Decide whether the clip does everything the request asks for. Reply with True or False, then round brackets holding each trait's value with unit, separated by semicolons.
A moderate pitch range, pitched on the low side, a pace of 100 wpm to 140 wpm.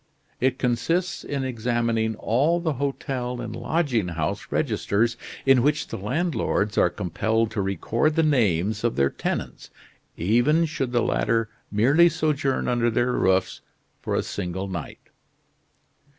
True (4.8 semitones; 120 Hz; 135 wpm)